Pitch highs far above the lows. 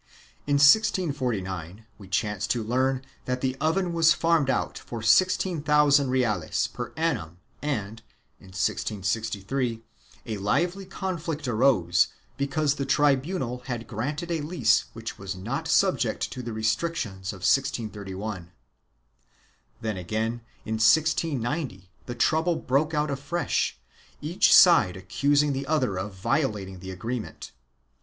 Yes: wide, 6.2 semitones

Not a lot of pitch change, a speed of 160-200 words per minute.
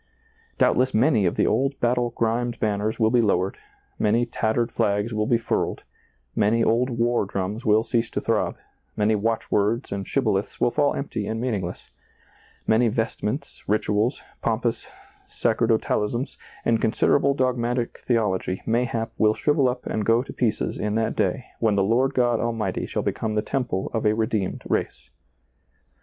Yes: narrow, 2.3 semitones; average, 165 wpm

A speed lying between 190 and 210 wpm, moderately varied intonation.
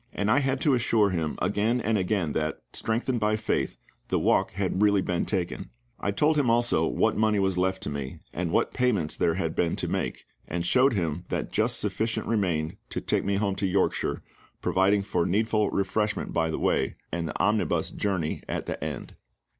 Yes: average, 195 wpm; average, 3.9 semitones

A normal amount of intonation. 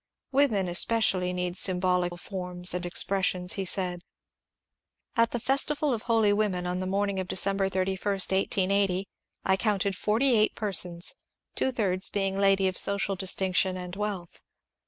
No: narrow, 2.1 semitones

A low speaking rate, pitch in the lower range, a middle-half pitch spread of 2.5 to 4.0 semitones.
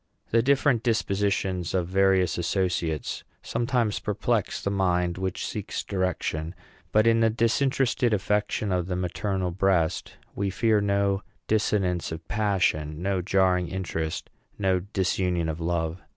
Yes: slow, 130 wpm; very low, 95 Hz; average, 2.8 semitones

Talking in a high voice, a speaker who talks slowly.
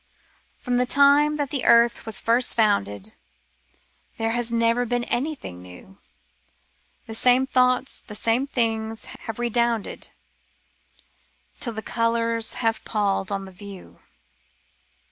Yes: high, 230 Hz; slow, 125 wpm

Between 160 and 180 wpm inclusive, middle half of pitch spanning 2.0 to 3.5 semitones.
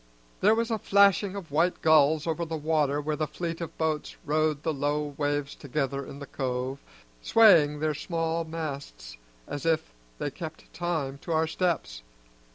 Yes: average, 165 wpm; narrow, 2.5 semitones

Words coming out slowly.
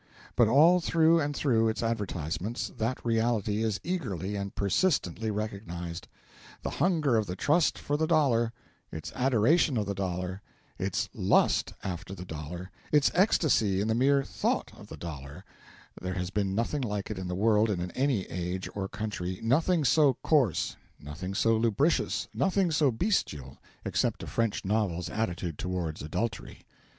No: average, 160 wpm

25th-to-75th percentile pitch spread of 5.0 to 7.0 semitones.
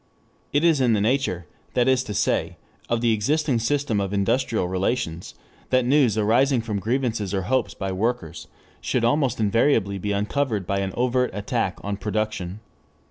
No: average, 4.2 semitones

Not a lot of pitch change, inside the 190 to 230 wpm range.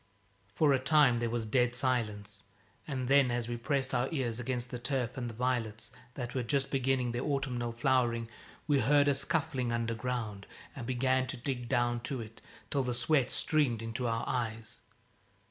No: narrow, 2.3 semitones; average, 180 wpm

